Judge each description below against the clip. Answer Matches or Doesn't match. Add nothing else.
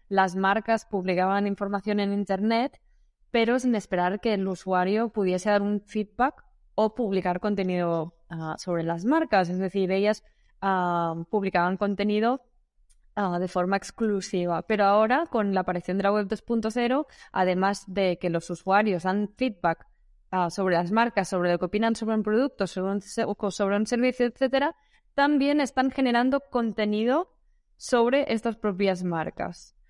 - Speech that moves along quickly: Doesn't match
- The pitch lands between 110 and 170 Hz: Doesn't match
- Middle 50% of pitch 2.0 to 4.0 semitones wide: Matches